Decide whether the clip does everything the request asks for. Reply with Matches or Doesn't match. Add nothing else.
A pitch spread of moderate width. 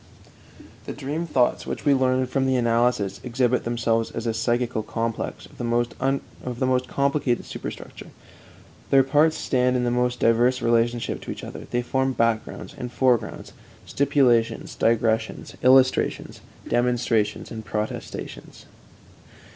Doesn't match